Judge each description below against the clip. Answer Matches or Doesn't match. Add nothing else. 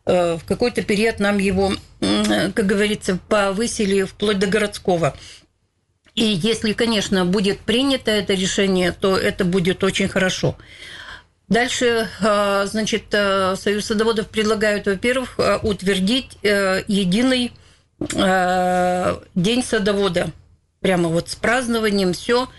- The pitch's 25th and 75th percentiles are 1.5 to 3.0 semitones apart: Matches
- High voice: Matches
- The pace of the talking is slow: Matches